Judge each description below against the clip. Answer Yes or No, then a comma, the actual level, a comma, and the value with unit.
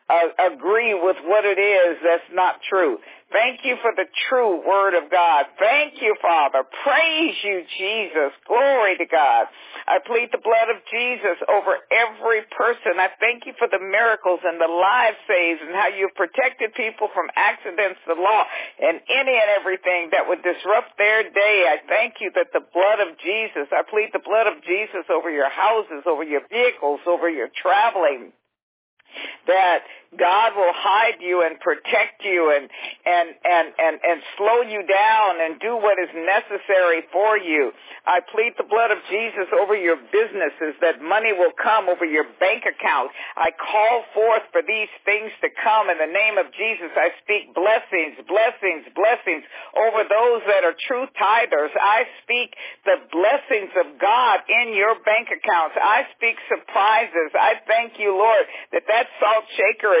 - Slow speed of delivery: No, average, 170 wpm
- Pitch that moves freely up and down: No, average, 4.3 semitones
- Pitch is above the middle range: Yes, high, 210 Hz